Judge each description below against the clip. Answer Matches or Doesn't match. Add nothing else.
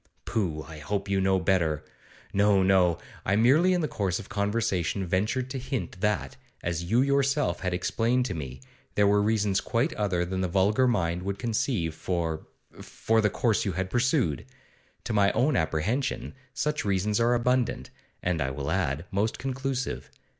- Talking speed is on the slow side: Doesn't match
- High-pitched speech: Doesn't match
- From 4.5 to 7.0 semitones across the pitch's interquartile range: Matches